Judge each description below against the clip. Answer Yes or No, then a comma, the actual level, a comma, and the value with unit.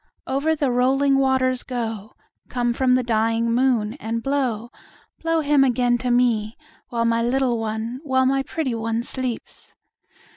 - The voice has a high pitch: Yes, high, 245 Hz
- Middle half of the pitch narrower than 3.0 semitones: Yes, narrow, 2.4 semitones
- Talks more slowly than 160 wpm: Yes, average, 150 wpm